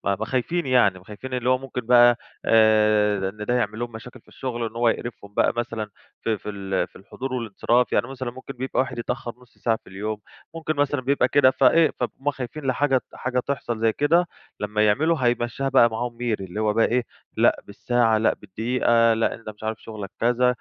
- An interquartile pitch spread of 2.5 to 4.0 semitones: Yes, average, 2.9 semitones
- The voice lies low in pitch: Yes, low, 120 Hz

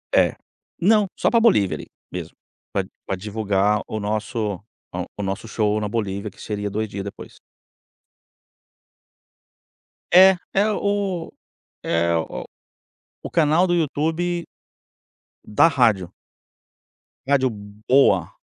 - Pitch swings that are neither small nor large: No, wide, 8.5 semitones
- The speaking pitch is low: Yes, low, 110 Hz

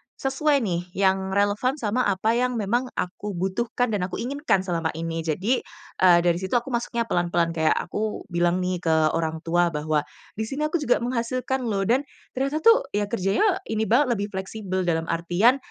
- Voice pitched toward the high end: Yes, high, 200 Hz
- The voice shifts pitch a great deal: Yes, wide, 5.8 semitones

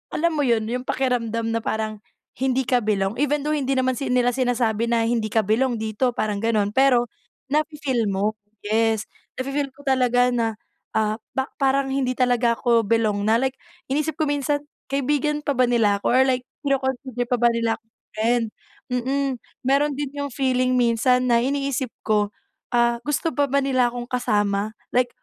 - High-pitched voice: Yes, very high, 250 Hz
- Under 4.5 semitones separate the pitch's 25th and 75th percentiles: Yes, average, 3.0 semitones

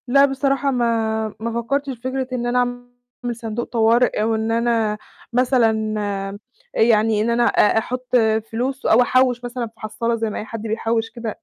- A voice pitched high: Yes, high, 235 Hz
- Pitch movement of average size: No, narrow, 1.9 semitones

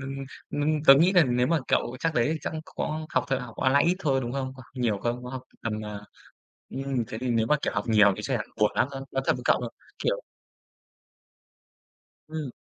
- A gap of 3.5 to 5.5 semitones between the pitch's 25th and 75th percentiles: Yes, average, 3.9 semitones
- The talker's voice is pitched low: Yes, low, 130 Hz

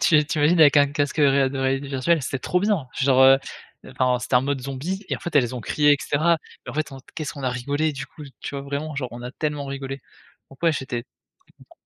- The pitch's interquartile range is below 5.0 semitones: Yes, narrow, 2.4 semitones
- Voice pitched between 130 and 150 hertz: Yes, medium, 140 Hz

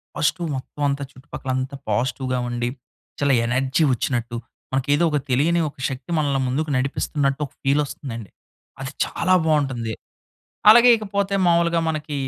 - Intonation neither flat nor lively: Yes, average, 3.5 semitones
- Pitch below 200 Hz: Yes, medium, 140 Hz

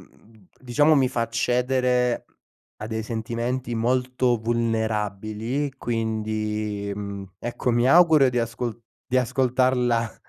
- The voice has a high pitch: No, low, 120 Hz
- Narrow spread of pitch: Yes, narrow, 2.3 semitones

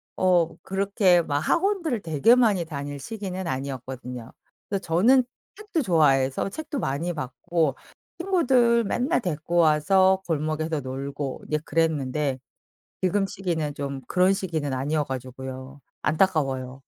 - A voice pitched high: No, medium, 160 Hz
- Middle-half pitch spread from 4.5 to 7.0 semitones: Yes, wide, 5.9 semitones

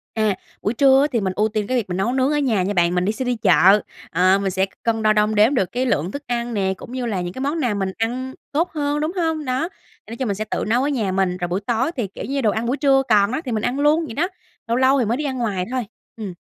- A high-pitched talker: Yes, high, 230 Hz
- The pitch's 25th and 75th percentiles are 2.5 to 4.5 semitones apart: No, average, 4.9 semitones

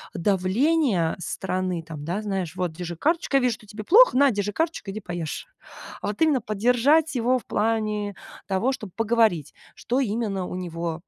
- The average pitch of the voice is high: Yes, high, 210 Hz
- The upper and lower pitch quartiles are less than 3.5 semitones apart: No, wide, 5.4 semitones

